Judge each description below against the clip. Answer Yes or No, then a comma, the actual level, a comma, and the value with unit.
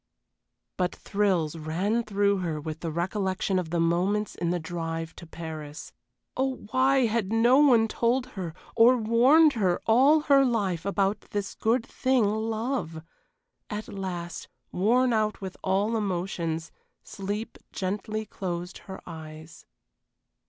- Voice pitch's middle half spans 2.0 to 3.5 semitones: No, average, 4.8 semitones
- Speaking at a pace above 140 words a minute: No, slow, 135 wpm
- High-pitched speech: Yes, high, 200 Hz